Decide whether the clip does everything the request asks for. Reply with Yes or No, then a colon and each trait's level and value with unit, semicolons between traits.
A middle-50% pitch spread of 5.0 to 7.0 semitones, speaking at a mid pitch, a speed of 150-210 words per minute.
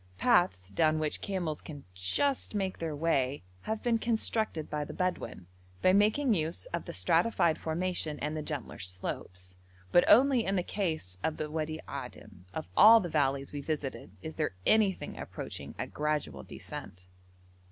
Yes: average, 5.3 semitones; medium, 155 Hz; average, 165 wpm